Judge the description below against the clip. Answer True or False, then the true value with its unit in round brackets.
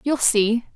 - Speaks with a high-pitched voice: True (235 Hz)